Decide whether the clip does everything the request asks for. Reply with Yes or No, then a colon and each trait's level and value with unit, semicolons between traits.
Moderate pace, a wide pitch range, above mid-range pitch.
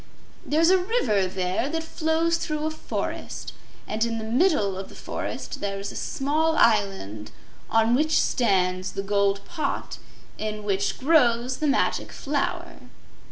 Yes: average, 150 wpm; wide, 7.8 semitones; high, 230 Hz